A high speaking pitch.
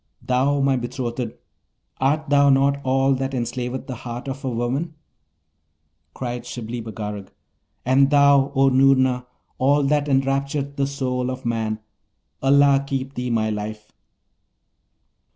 No: low, 130 Hz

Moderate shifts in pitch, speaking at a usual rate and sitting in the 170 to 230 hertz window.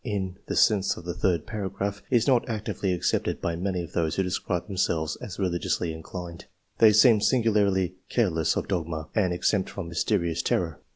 No: average, 3.3 semitones; average, 180 wpm; very low, 95 Hz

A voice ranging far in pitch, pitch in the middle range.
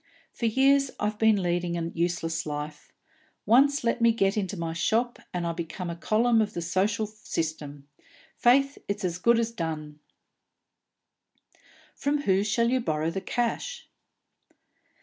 No: wide, 5.7 semitones; high, 200 Hz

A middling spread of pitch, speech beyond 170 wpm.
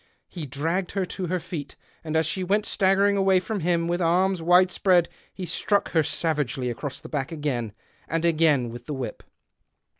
Yes: average, 3.9 semitones; average, 185 wpm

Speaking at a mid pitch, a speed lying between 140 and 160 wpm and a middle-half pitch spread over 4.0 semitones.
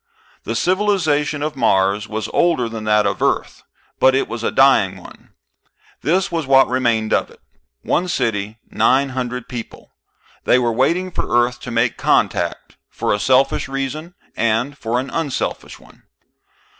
No: low, 130 Hz; average, 155 wpm; average, 4.4 semitones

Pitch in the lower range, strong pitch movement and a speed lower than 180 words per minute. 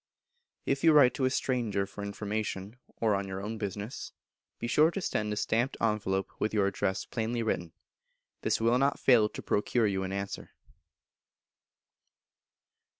No: low, 110 Hz; average, 3.5 semitones; average, 155 wpm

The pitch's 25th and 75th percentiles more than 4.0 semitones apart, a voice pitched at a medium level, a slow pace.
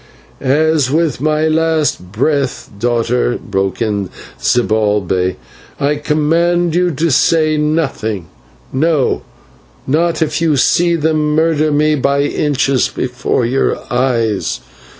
Yes: average, 4.5 semitones; medium, 145 Hz; slow, 110 wpm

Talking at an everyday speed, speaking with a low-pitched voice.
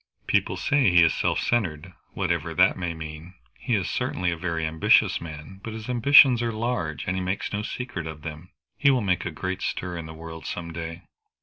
No: fast, 210 wpm; very low, 90 Hz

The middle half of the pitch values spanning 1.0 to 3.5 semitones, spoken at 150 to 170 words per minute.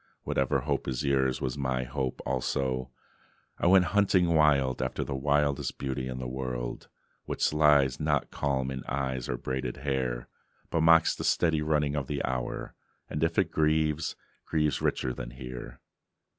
Yes: average, 3.0 semitones; average, 160 wpm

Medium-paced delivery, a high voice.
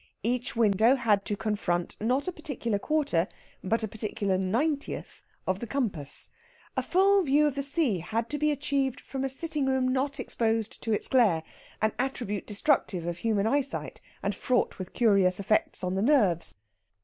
Yes: average, 175 wpm; high, 230 Hz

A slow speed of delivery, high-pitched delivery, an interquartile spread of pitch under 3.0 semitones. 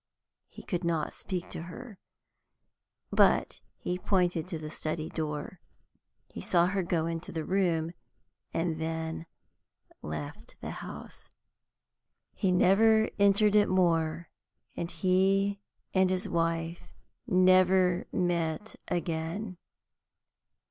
No: slow, 110 wpm; medium, 175 Hz; narrow, 2.5 semitones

